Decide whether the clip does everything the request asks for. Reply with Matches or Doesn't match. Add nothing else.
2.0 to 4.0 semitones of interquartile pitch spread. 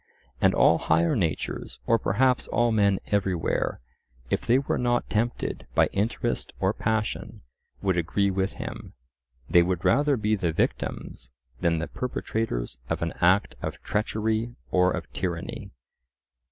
Doesn't match